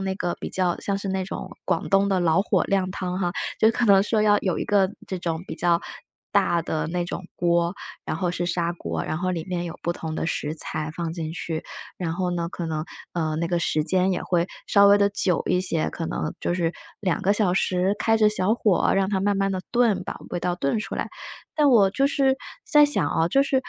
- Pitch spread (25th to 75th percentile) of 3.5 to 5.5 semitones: No, average, 2.9 semitones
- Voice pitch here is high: No, medium, 180 Hz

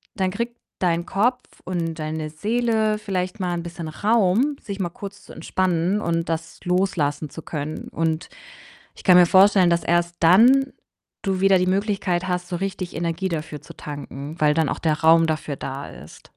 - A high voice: No, medium, 175 Hz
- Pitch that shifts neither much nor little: Yes, average, 3.3 semitones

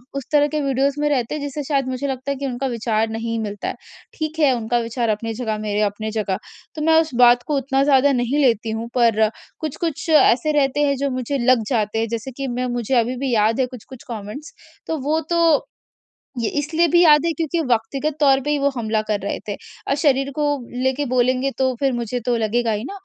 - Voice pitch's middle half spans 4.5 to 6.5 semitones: No, average, 3.8 semitones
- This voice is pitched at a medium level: No, very high, 255 Hz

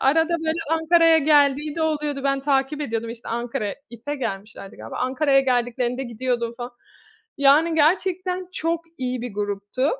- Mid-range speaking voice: No, very high, 275 Hz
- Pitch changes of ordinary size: Yes, average, 4.7 semitones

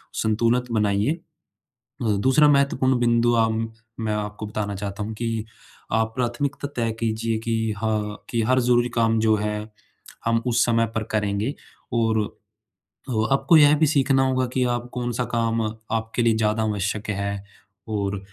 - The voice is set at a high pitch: No, low, 115 Hz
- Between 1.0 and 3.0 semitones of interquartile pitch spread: Yes, narrow, 2.4 semitones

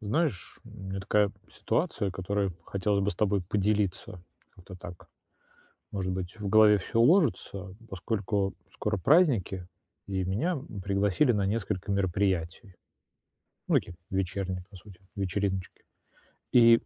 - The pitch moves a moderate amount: No, narrow, 2.1 semitones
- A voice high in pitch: No, low, 100 Hz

